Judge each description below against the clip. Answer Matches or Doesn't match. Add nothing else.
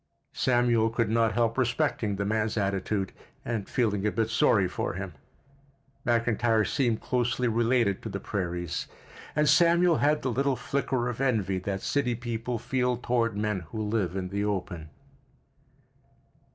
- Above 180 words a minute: Doesn't match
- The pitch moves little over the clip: Doesn't match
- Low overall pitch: Matches